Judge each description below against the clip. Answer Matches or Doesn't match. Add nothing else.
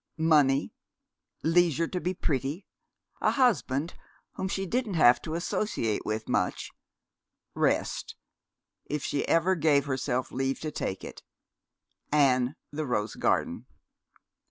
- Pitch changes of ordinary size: Matches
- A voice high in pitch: Doesn't match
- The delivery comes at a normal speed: Doesn't match